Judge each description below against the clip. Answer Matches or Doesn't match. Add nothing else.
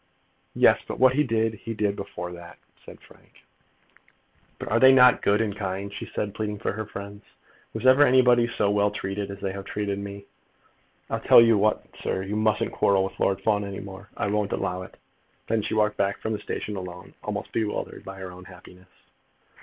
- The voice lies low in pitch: Matches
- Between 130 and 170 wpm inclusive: Doesn't match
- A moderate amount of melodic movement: Doesn't match